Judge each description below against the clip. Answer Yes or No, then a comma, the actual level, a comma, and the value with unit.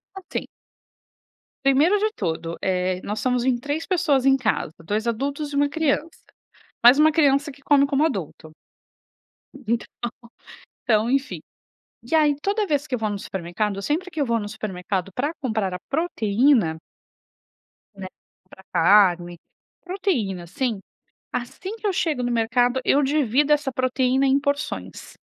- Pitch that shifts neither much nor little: No, wide, 5.9 semitones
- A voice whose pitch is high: Yes, very high, 260 Hz